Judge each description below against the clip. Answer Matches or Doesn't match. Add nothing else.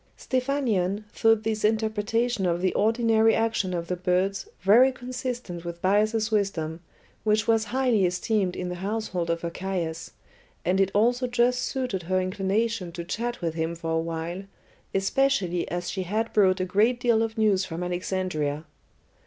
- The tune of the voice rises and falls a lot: Doesn't match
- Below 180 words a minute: Matches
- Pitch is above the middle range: Matches